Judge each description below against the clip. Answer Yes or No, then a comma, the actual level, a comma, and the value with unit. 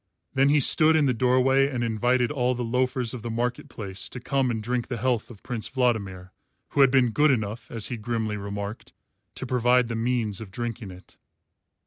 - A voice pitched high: No, low, 120 Hz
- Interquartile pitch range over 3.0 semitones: No, narrow, 2.6 semitones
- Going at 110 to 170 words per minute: No, average, 200 wpm